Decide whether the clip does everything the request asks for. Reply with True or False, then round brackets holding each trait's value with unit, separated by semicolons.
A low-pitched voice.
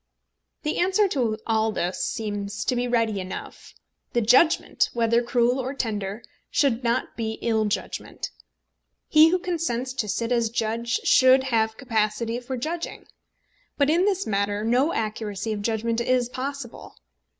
False (235 Hz)